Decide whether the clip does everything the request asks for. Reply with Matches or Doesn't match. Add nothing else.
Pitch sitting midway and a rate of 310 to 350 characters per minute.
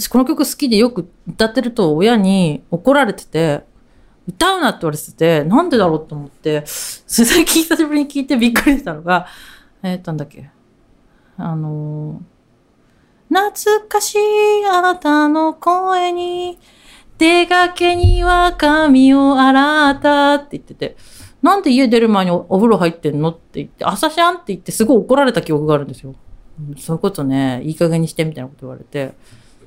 Doesn't match